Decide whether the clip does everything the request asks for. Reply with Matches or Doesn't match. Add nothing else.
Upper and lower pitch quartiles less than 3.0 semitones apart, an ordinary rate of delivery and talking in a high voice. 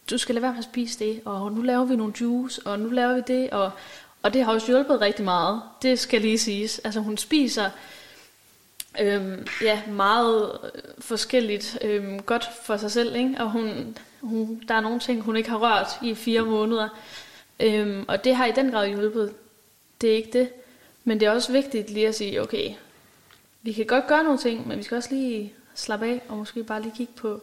Matches